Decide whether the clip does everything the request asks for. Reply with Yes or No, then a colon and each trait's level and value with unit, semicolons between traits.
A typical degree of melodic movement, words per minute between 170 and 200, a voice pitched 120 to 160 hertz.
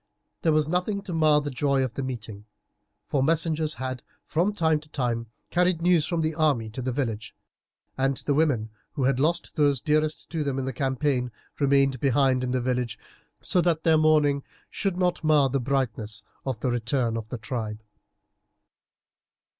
Yes: average, 4.0 semitones; average, 180 wpm; medium, 140 Hz